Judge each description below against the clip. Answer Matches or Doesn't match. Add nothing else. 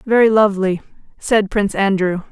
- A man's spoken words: Doesn't match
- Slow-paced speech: Matches